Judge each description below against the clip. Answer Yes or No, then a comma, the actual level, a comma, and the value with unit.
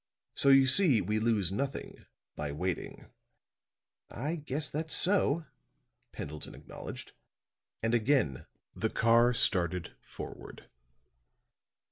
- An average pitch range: No, wide, 7.5 semitones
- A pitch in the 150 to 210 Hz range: No, low, 120 Hz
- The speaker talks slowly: Yes, slow, 100 wpm